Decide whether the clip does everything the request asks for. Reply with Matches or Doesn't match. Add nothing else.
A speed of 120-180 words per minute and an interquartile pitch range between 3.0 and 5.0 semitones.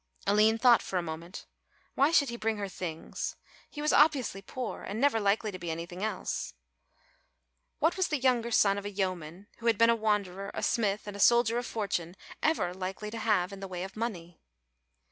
Doesn't match